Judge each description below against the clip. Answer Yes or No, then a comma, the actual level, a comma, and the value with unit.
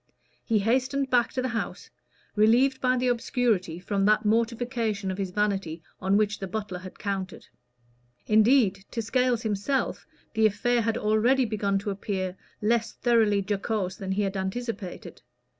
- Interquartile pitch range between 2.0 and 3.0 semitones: No, average, 3.4 semitones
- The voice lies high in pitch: Yes, high, 215 Hz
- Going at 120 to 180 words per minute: Yes, average, 155 wpm